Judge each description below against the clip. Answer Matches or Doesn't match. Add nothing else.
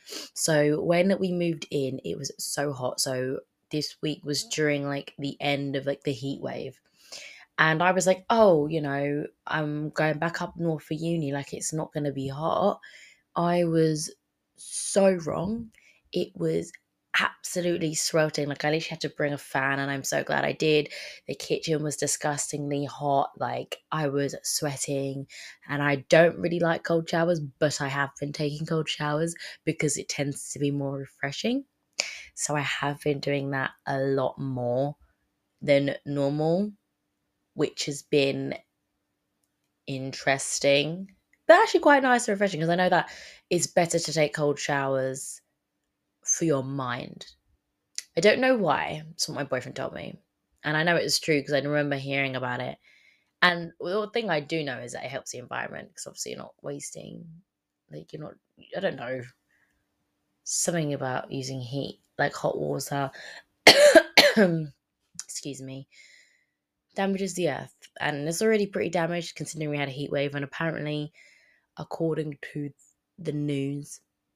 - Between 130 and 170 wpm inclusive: Matches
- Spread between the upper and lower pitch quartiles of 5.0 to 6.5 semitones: Doesn't match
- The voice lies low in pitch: Doesn't match